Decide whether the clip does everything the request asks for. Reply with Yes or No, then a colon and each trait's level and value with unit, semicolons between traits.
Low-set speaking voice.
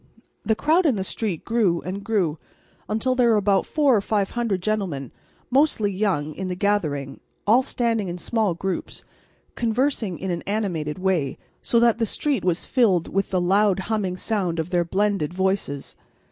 No: high, 200 Hz